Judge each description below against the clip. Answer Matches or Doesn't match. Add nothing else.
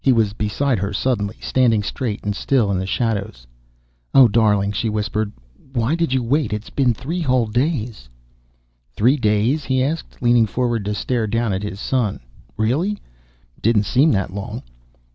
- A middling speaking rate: Matches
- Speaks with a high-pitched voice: Doesn't match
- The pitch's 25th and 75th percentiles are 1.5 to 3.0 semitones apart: Doesn't match